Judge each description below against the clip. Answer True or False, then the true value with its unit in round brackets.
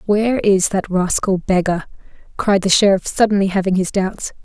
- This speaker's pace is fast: False (160 wpm)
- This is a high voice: True (195 Hz)